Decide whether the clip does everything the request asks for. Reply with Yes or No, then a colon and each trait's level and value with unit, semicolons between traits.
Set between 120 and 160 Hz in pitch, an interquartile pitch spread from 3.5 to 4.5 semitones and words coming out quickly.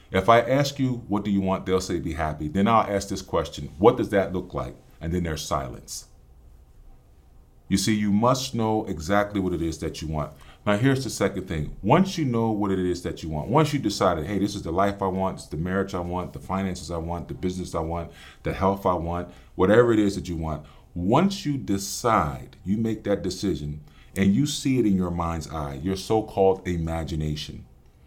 No: very low, 95 Hz; average, 4.2 semitones; fast, 220 wpm